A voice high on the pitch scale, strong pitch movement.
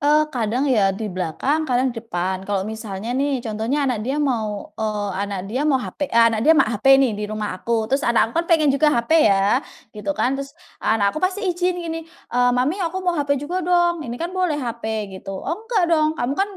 Yes: very high, 250 Hz; wide, 6.0 semitones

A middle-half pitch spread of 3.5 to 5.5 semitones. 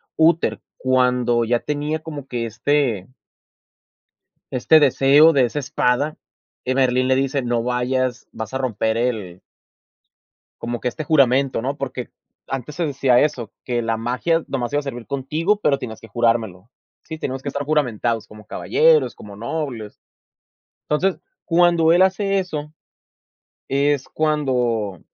Yes: average, 4.0 semitones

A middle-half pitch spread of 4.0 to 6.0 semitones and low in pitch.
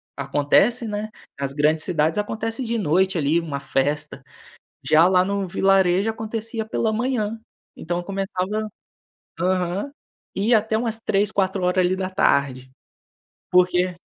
No: average, 4.3 semitones; high, 190 Hz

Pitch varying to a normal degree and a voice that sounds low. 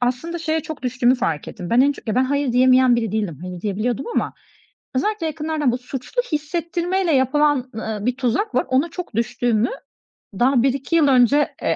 No: average, 3.9 semitones; very high, 260 Hz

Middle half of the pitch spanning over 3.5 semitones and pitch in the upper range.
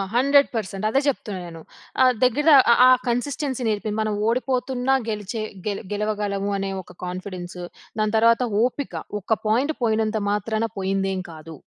Yes: average, 4.2 semitones; high, 215 Hz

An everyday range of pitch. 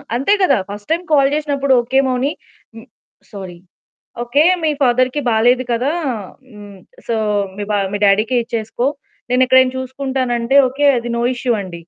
Yes: average, 3.0 semitones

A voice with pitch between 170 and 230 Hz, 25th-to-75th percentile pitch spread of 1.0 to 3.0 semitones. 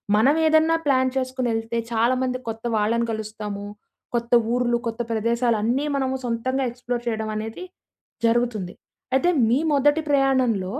No: high, 240 Hz; average, 2.7 semitones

